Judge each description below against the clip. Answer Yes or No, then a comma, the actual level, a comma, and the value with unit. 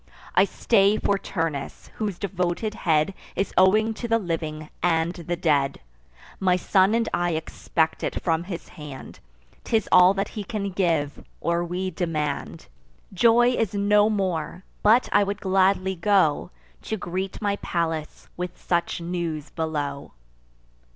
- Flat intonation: No, average, 3.6 semitones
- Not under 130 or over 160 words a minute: Yes, average, 145 wpm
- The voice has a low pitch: No, medium, 180 Hz